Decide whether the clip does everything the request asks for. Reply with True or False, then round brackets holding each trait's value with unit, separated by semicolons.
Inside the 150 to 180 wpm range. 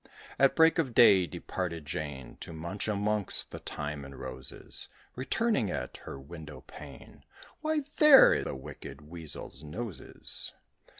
False (135 wpm)